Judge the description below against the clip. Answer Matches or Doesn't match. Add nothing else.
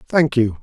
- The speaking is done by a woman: Doesn't match